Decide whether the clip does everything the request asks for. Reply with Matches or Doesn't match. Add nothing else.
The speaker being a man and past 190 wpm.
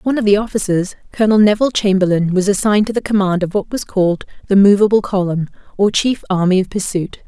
Doesn't match